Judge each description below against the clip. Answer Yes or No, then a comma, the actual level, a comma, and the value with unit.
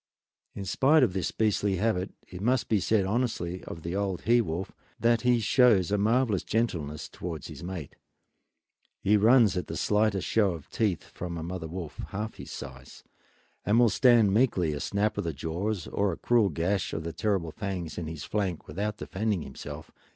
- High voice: No, very low, 95 Hz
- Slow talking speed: No, average, 185 wpm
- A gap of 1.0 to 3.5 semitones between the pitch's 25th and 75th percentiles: No, average, 4.4 semitones